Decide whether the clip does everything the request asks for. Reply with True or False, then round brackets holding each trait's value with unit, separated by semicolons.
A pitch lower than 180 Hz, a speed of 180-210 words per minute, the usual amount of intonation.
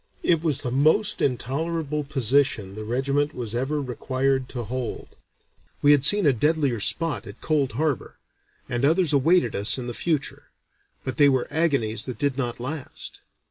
False (135 Hz; 165 wpm; 3.7 semitones)